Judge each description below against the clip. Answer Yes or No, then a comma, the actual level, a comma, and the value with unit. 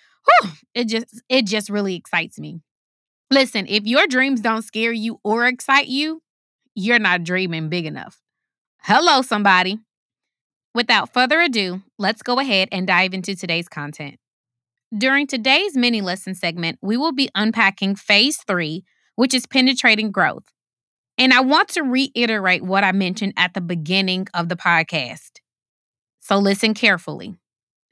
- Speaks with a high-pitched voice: Yes, high, 210 Hz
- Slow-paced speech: No, average, 145 wpm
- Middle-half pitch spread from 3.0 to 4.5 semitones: No, average, 5.3 semitones